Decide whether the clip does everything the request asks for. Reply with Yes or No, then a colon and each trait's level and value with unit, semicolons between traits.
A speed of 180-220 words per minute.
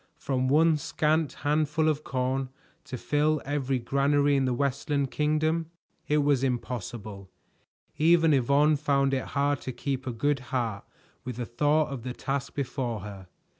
No: average, 155 wpm